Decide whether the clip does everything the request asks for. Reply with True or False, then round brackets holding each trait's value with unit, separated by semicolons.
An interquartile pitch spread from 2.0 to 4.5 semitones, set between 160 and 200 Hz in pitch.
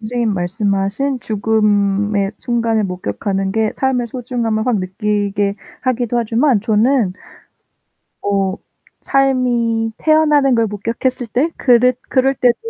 False (3.7 semitones; 225 Hz)